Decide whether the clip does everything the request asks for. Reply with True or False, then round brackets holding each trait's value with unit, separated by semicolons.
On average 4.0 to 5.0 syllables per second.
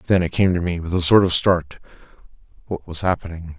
False (5.9 syllables/s)